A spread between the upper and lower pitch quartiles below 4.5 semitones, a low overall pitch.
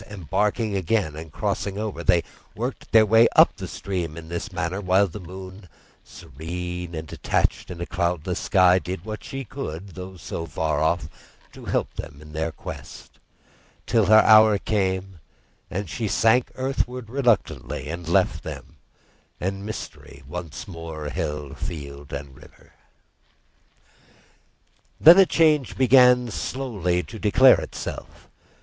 No: average, 4.8 semitones; very low, 95 Hz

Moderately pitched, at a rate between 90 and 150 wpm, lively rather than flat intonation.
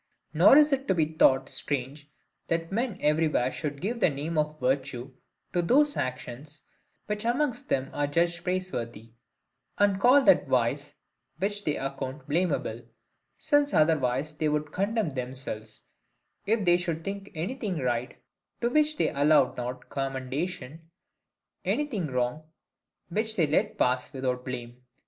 Yes: medium, 155 Hz; average, 140 wpm; wide, 7.0 semitones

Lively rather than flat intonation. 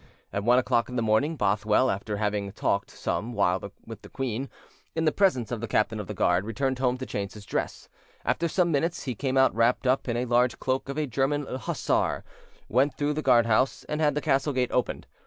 No: average, 4.1 semitones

